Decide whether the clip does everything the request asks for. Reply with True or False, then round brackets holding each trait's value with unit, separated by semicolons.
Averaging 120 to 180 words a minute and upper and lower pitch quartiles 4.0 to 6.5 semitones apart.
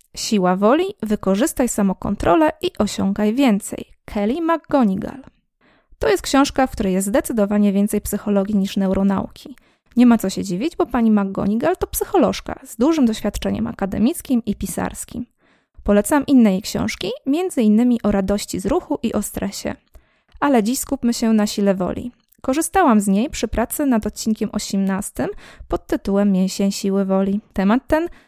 True (150 wpm; 5.1 semitones)